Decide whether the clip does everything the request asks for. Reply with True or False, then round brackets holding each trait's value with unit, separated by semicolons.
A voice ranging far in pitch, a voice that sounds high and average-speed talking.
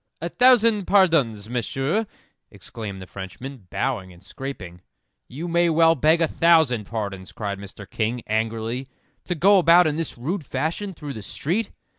False (7.7 semitones; 135 Hz; 155 wpm)